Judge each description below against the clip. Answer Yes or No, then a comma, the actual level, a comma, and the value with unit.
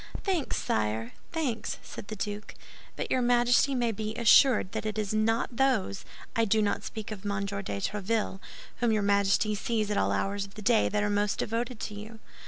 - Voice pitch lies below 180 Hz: No, high, 215 Hz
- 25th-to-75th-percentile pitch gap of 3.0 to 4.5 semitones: No, narrow, 2.4 semitones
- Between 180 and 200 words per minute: Yes, average, 190 wpm